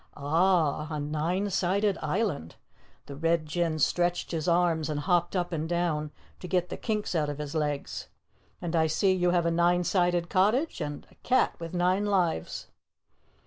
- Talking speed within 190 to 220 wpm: No, average, 175 wpm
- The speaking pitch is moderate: Yes, medium, 175 Hz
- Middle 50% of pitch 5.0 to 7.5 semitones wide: No, average, 2.8 semitones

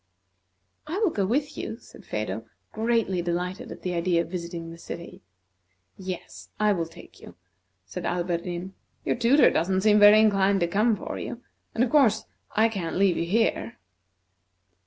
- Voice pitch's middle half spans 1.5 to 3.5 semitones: No, average, 4.4 semitones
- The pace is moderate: Yes, average, 160 wpm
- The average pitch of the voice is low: No, high, 190 Hz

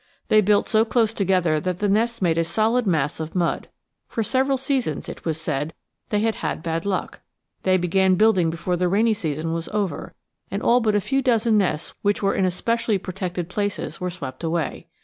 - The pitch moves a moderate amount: Yes, average, 4.5 semitones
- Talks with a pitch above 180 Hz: Yes, high, 190 Hz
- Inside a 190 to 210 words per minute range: Yes, average, 195 wpm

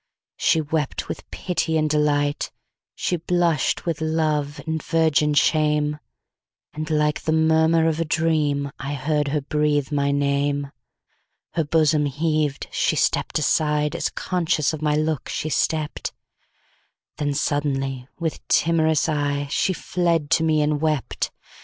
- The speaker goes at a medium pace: No, slow, 115 wpm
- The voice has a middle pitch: Yes, medium, 150 Hz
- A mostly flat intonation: Yes, narrow, 1.6 semitones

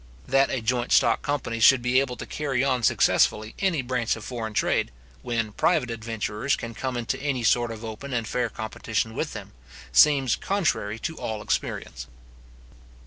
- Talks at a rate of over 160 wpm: Yes, average, 170 wpm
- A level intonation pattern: No, average, 3.2 semitones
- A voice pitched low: Yes, low, 120 Hz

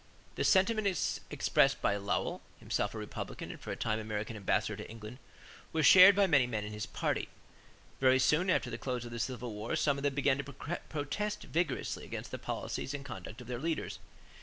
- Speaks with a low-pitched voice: Yes, low, 130 Hz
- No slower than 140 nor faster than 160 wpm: No, fast, 205 wpm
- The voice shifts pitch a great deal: Yes, wide, 5.7 semitones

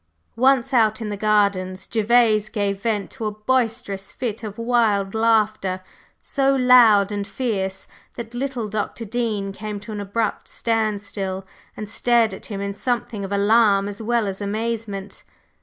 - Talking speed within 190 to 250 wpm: No, average, 155 wpm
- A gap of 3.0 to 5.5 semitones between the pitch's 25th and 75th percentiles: No, narrow, 2.5 semitones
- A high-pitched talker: Yes, high, 215 Hz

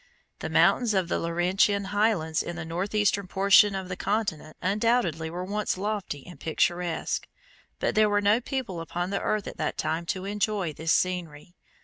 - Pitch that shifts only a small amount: No, average, 3.4 semitones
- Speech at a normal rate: Yes, average, 170 wpm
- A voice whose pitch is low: No, high, 190 Hz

